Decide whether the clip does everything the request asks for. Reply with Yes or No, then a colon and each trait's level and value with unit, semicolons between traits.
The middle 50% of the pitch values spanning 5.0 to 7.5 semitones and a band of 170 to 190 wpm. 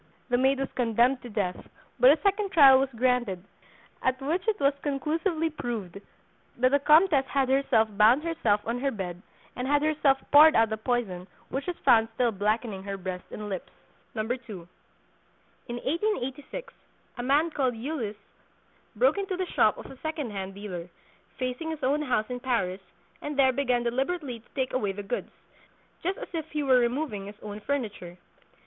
Yes: average, 5.3 semitones; average, 175 wpm